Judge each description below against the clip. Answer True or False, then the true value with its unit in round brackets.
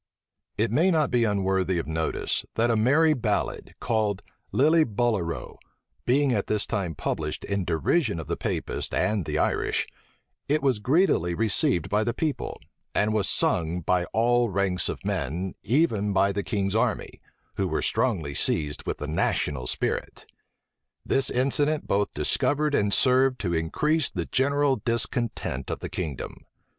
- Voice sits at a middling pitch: False (105 Hz)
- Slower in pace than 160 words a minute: True (150 wpm)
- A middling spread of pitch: False (6.4 semitones)